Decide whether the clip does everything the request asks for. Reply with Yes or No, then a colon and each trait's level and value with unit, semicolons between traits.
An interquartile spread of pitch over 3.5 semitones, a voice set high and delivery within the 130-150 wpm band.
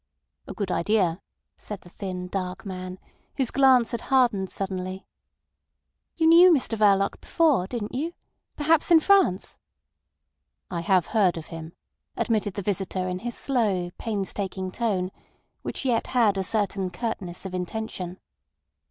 Yes: average, 4.6 semitones; high, 200 Hz; slow, 135 wpm